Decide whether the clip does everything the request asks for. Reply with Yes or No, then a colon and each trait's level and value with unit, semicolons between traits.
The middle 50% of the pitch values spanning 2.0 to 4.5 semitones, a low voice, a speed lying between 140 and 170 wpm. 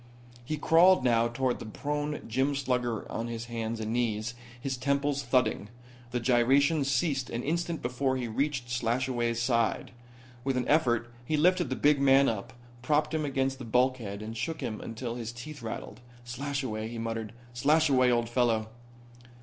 Yes: average, 3.2 semitones; low, 125 Hz; average, 165 wpm